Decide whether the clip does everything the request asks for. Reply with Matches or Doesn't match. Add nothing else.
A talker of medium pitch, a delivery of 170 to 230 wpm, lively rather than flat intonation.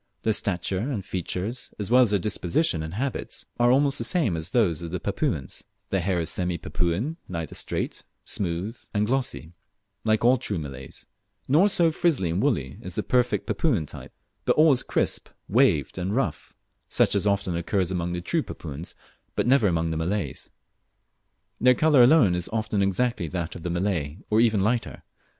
Doesn't match